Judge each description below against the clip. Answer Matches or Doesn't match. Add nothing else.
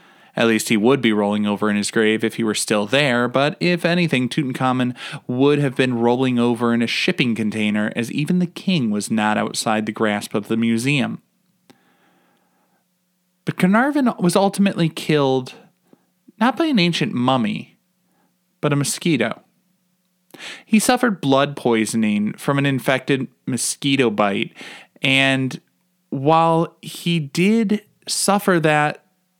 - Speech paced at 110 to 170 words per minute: Matches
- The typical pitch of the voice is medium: Matches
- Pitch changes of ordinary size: Doesn't match